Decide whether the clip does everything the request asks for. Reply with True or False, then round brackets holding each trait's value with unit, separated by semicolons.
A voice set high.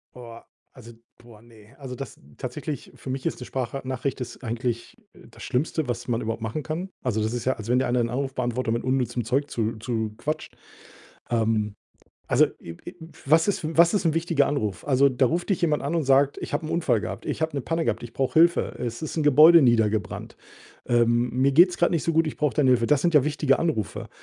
False (130 Hz)